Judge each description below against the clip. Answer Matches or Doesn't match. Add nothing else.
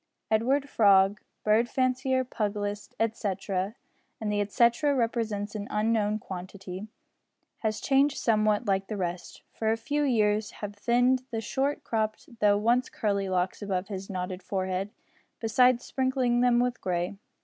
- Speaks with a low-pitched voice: Doesn't match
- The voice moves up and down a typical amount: Matches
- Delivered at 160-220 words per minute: Doesn't match